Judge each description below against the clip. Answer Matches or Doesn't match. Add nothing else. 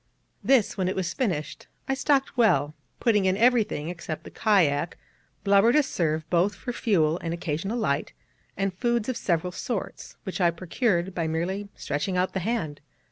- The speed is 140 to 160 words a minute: Doesn't match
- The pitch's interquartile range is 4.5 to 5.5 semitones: Matches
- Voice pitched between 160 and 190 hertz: Matches